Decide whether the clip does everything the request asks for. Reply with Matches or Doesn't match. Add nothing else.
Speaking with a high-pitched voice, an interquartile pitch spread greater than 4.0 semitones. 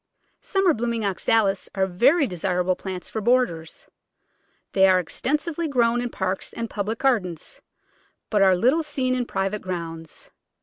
Matches